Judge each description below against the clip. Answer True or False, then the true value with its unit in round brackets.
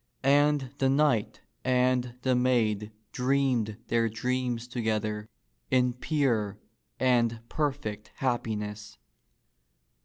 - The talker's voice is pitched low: True (125 Hz)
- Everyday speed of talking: False (95 wpm)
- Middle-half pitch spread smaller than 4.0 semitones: True (3.1 semitones)